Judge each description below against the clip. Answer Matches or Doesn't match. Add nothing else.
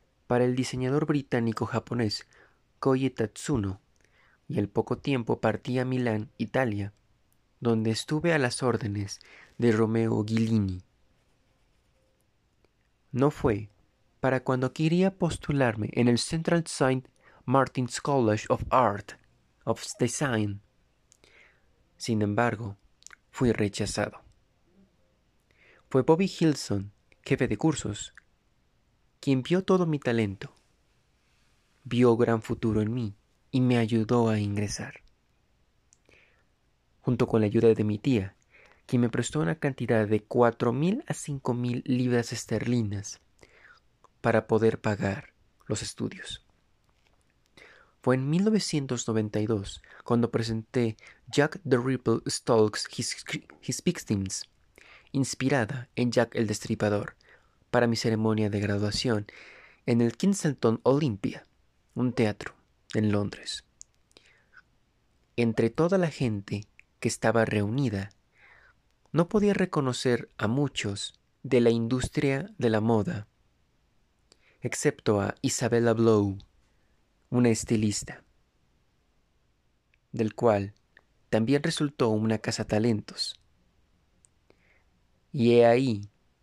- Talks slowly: Matches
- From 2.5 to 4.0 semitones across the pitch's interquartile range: Matches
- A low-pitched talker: Matches